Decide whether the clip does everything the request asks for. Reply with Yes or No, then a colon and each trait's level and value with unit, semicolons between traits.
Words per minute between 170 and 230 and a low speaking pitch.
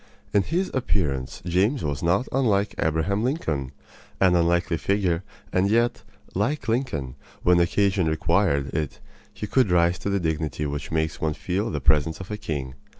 No: average, 160 wpm; very low, 90 Hz